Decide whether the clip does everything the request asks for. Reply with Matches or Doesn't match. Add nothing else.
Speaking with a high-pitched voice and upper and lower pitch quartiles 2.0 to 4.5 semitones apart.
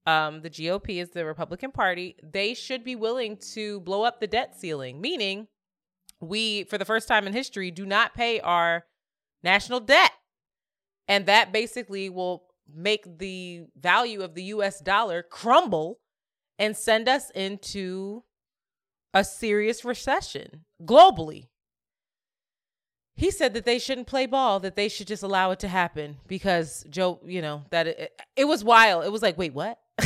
Matches